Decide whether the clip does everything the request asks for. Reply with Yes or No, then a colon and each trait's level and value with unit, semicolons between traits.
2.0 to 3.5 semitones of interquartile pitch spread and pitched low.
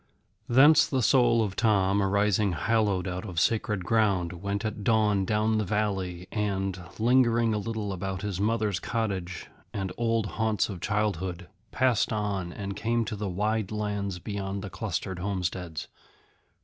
Yes: narrow, 2.5 semitones; low, 105 Hz